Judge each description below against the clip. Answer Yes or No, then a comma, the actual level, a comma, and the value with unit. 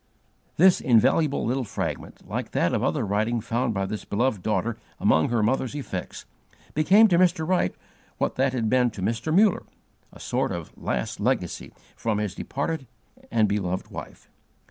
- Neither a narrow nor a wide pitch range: No, wide, 5.7 semitones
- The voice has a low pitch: Yes, low, 120 Hz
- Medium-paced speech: Yes, average, 160 wpm